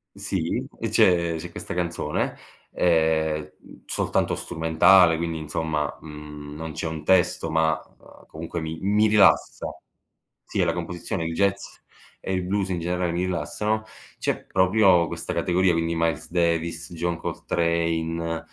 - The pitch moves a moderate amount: No, narrow, 2.0 semitones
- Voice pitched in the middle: No, very low, 85 Hz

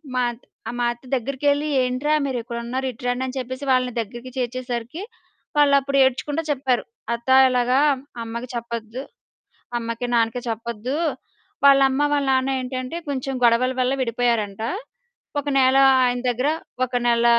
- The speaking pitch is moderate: No, very high, 250 Hz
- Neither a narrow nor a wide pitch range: No, narrow, 2.1 semitones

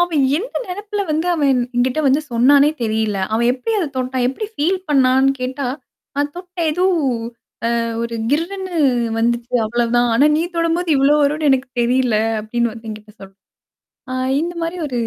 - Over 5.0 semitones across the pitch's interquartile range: Yes, wide, 5.6 semitones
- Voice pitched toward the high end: Yes, very high, 270 Hz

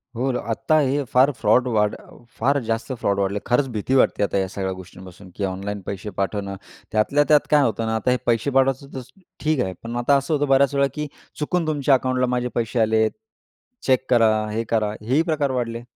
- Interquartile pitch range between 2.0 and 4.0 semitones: No, average, 4.5 semitones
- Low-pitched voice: Yes, low, 120 Hz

